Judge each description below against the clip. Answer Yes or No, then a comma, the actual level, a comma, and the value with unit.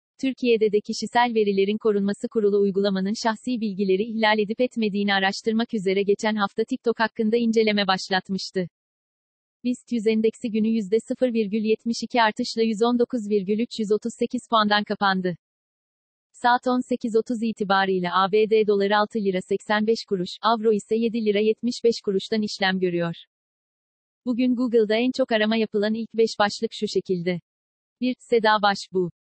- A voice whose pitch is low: No, high, 220 Hz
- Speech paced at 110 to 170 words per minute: Yes, average, 125 wpm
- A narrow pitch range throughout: Yes, narrow, 2.3 semitones